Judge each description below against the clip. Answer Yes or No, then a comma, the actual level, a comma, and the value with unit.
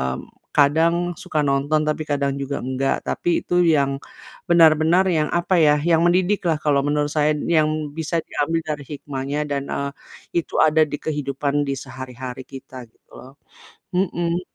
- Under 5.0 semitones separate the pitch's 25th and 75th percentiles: Yes, average, 2.8 semitones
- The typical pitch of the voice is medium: Yes, medium, 150 Hz